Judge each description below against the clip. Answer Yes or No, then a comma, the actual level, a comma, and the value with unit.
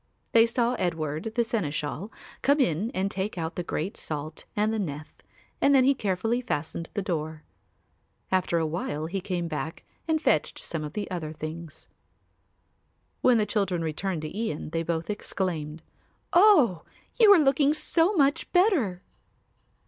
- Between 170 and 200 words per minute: No, average, 155 wpm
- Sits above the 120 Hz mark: Yes, medium, 185 Hz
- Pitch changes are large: Yes, wide, 6.7 semitones